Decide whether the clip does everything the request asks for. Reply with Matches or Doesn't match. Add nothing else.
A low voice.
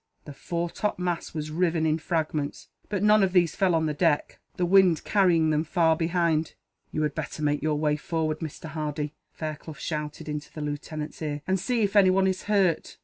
Doesn't match